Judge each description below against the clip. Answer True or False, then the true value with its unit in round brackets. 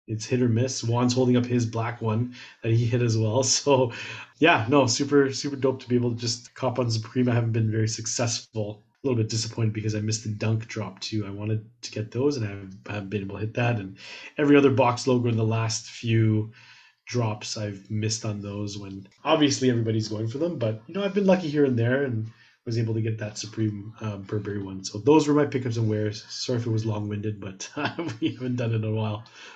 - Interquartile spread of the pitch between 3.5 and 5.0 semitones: False (2.6 semitones)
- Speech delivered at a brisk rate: True (245 wpm)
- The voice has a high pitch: False (115 Hz)